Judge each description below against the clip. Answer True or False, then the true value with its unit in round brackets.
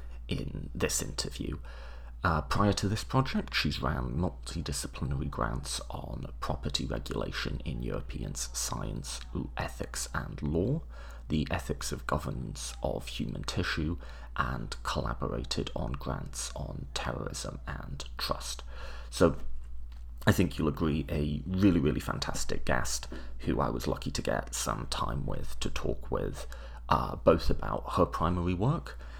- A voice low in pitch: True (65 Hz)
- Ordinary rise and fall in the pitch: True (4.4 semitones)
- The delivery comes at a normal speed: False (130 wpm)